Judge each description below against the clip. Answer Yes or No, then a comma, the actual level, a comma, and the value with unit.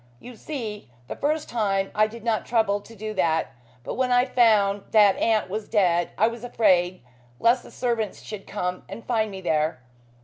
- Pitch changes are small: No, average, 3.2 semitones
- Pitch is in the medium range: No, high, 215 Hz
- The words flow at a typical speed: Yes, average, 190 wpm